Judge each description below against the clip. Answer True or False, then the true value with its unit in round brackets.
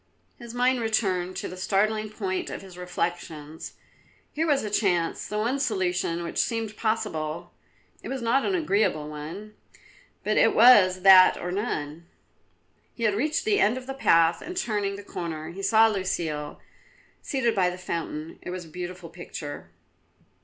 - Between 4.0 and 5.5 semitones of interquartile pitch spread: True (4.6 semitones)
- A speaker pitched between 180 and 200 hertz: True (190 Hz)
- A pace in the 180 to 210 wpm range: False (160 wpm)